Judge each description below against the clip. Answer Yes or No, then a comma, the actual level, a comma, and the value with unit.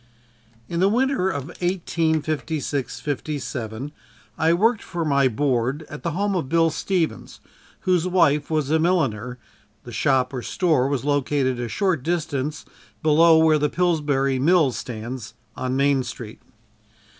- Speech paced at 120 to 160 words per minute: Yes, average, 140 wpm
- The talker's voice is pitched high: No, medium, 150 Hz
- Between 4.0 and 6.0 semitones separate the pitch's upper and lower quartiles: Yes, average, 4.3 semitones